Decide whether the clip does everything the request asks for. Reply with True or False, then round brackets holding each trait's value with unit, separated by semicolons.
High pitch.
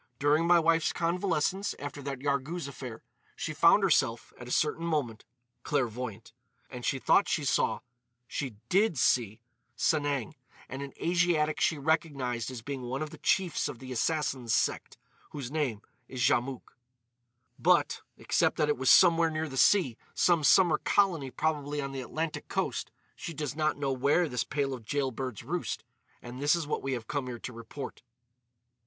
False (140 Hz)